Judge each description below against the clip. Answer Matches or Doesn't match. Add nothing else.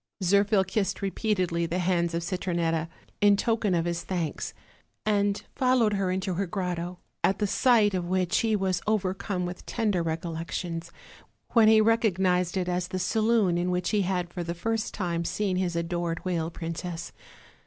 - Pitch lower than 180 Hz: Doesn't match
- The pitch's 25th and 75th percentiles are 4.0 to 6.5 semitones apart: Doesn't match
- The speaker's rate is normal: Matches